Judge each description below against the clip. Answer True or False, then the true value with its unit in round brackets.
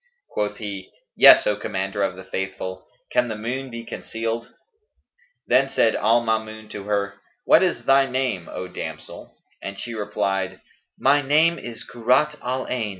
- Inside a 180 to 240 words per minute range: False (155 wpm)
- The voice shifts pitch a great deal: False (4.1 semitones)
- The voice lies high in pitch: False (110 Hz)